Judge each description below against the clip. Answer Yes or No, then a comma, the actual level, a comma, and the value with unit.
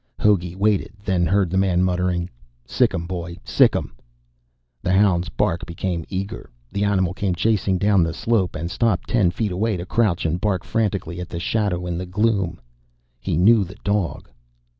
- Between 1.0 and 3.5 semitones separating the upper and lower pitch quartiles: Yes, average, 2.7 semitones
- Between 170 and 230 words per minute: Yes, average, 180 wpm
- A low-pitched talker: Yes, very low, 95 Hz